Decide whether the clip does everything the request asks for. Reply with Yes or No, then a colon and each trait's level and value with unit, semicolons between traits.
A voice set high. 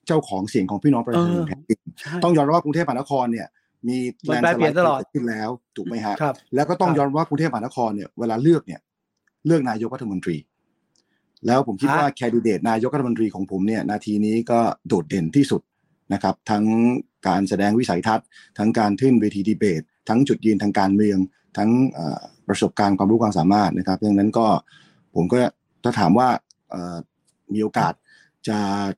No: low, 110 Hz